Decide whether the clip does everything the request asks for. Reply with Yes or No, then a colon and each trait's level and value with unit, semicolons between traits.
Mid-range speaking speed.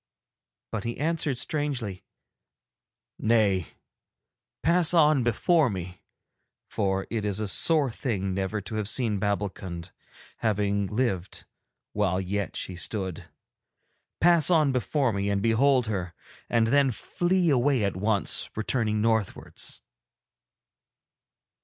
No: slow, 115 wpm